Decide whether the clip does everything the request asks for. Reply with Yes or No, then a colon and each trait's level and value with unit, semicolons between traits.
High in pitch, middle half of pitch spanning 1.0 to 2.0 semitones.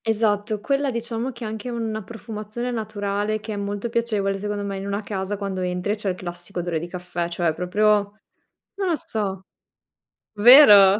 No: high, 205 Hz; narrow, 2.4 semitones